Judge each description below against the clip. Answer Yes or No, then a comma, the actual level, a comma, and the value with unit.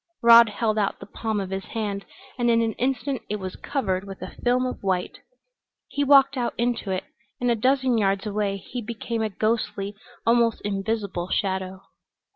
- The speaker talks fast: No, average, 180 wpm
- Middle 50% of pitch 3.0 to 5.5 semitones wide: Yes, average, 3.3 semitones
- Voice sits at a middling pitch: No, high, 220 Hz